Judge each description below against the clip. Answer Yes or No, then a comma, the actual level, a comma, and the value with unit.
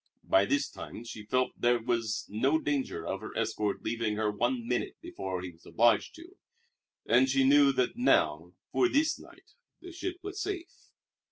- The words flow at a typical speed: Yes, average, 180 wpm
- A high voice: No, low, 125 Hz